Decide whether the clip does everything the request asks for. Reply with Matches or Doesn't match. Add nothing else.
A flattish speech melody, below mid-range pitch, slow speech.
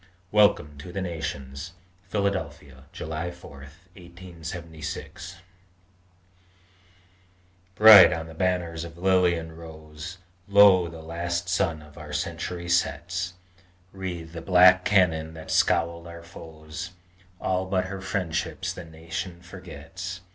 Matches